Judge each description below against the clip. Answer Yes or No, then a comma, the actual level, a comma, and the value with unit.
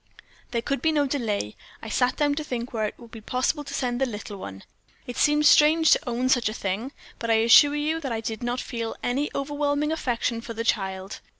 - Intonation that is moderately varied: Yes, average, 4.3 semitones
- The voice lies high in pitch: Yes, high, 245 Hz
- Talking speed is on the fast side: Yes, fast, 225 wpm